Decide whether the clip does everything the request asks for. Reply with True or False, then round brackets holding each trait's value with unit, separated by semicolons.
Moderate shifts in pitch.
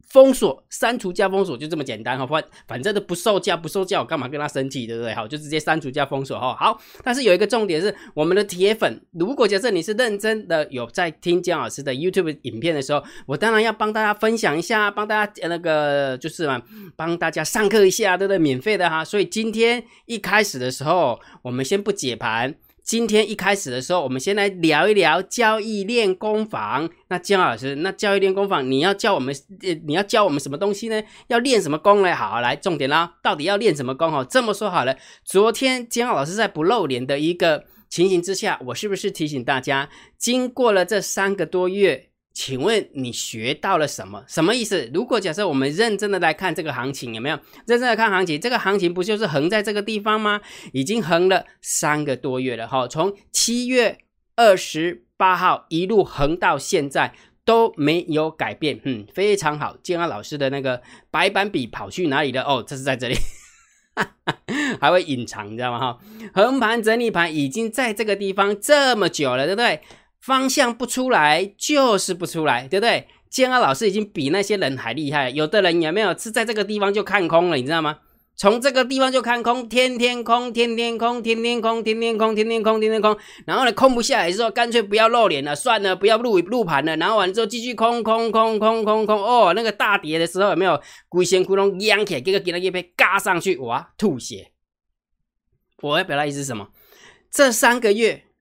False (6.4 semitones)